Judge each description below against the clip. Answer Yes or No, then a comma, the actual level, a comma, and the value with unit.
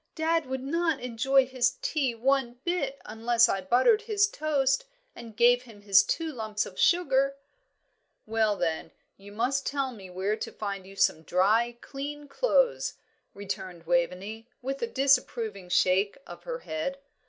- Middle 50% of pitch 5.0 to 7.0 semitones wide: Yes, wide, 5.4 semitones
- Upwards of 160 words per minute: No, average, 155 wpm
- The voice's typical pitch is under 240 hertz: No, high, 245 Hz